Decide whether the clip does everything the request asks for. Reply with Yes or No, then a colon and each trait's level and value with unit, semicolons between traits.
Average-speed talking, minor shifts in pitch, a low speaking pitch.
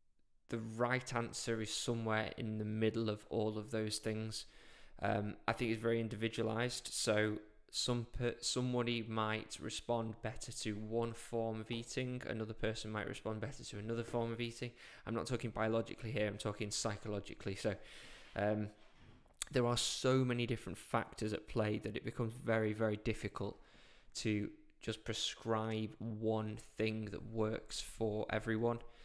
Yes: average, 155 wpm; narrow, 1.6 semitones; low, 110 Hz